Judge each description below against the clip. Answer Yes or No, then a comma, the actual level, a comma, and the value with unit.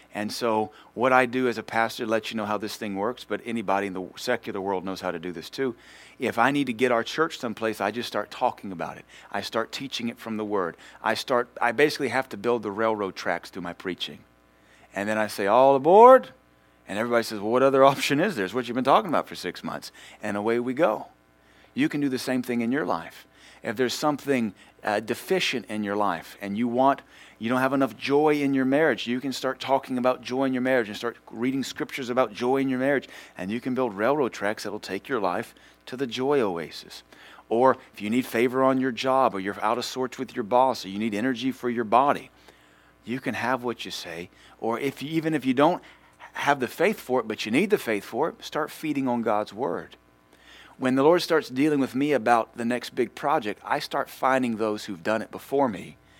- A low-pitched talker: Yes, low, 120 Hz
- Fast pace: Yes, fast, 240 wpm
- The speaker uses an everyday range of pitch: Yes, average, 3.9 semitones